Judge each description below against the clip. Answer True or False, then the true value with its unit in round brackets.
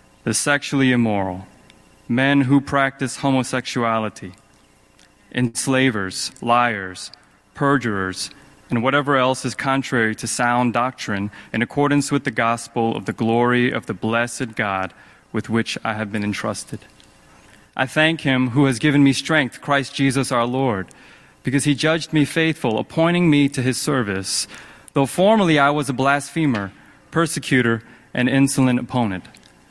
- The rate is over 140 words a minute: False (135 wpm)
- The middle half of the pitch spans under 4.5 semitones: True (3.7 semitones)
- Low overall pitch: True (130 Hz)